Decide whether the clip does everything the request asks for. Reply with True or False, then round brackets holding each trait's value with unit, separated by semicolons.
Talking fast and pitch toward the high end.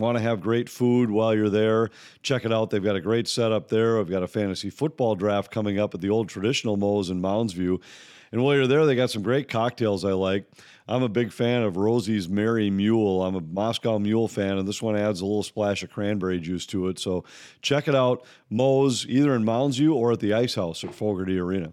False (230 wpm; 110 Hz)